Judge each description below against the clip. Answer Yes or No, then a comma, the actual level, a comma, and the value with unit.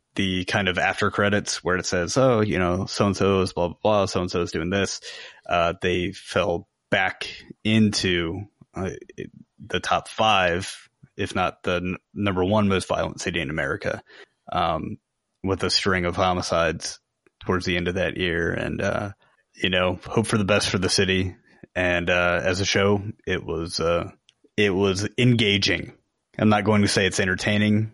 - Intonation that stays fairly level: Yes, narrow, 2.3 semitones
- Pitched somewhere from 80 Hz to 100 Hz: Yes, very low, 95 Hz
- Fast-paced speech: No, average, 185 wpm